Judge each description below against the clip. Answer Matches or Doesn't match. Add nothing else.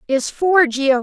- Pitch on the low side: Doesn't match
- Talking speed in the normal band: Matches